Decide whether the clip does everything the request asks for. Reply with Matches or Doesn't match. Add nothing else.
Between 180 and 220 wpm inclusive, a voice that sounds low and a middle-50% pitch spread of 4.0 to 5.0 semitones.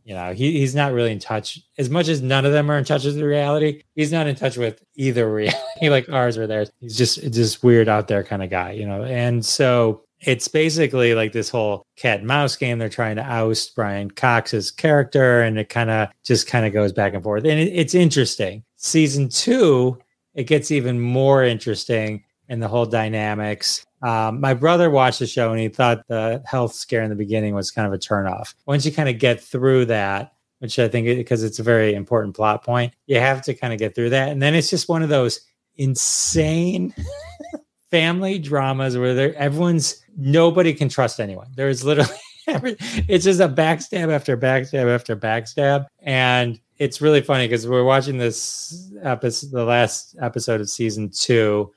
Matches